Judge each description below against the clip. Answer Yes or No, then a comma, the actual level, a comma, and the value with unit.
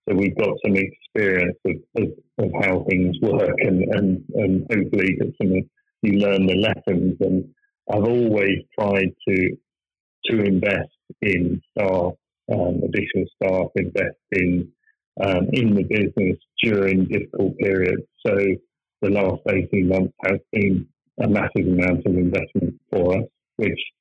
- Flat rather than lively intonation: Yes, narrow, 1.8 semitones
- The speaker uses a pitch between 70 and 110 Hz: Yes, very low, 95 Hz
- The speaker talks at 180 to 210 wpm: No, average, 145 wpm